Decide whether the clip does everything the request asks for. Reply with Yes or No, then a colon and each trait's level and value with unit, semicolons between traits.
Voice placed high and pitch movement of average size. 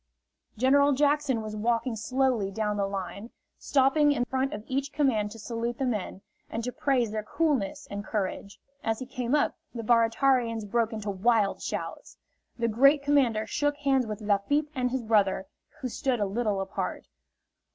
Yes: high, 235 Hz; average, 4.1 semitones